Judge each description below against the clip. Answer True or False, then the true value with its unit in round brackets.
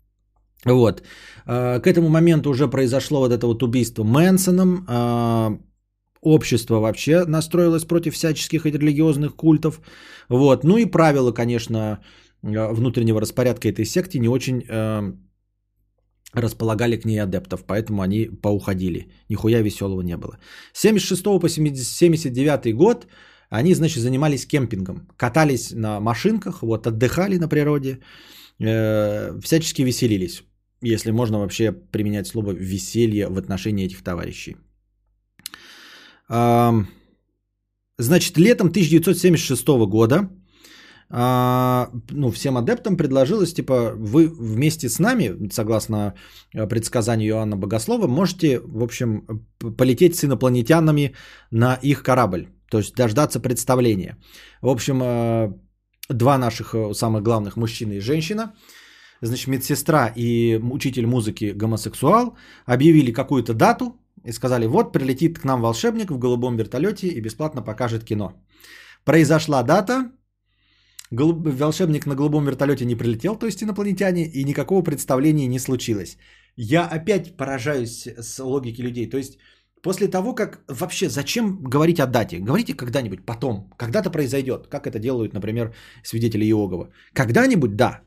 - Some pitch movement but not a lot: False (5.9 semitones)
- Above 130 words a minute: False (120 wpm)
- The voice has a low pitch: True (125 Hz)